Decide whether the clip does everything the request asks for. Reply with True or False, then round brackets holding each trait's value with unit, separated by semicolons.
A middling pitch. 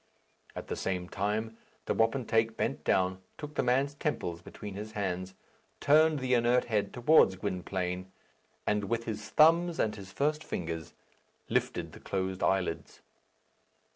False (105 Hz)